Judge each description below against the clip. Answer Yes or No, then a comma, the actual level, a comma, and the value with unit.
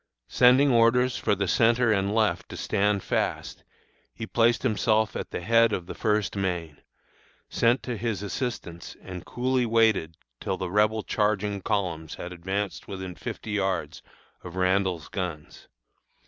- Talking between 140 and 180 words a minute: Yes, average, 150 wpm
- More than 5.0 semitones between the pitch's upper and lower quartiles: No, average, 3.8 semitones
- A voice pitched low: Yes, low, 105 Hz